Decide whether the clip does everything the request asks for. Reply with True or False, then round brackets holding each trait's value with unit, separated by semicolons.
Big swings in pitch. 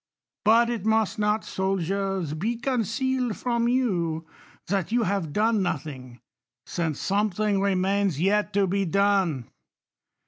False (3.8 semitones)